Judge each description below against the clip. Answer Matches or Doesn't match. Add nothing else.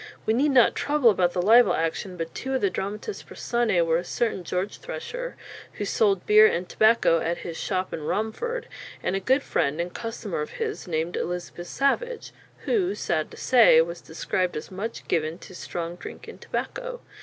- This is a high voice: Matches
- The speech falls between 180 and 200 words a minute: Matches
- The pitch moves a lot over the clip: Matches